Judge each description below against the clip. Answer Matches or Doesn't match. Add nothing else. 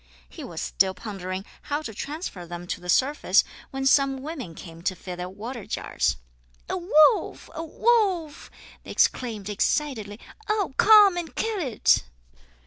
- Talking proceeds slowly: Doesn't match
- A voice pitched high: Matches